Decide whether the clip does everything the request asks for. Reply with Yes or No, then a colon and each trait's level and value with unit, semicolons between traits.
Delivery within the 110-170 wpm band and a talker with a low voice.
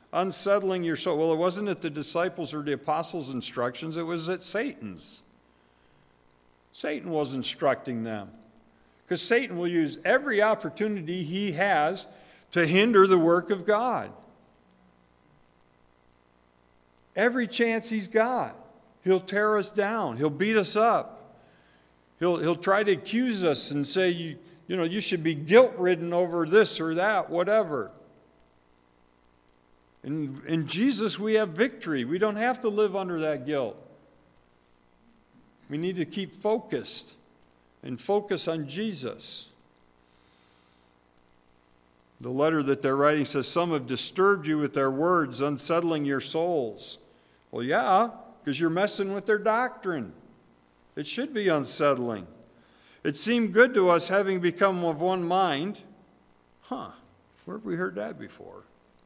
No: slow, 135 wpm; medium, 160 Hz